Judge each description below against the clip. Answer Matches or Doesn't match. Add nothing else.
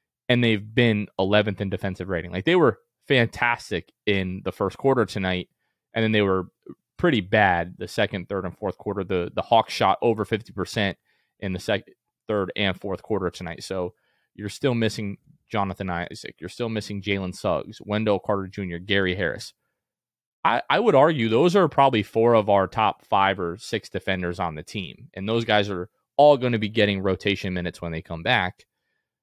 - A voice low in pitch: Matches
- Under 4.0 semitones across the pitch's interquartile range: Matches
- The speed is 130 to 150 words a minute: Doesn't match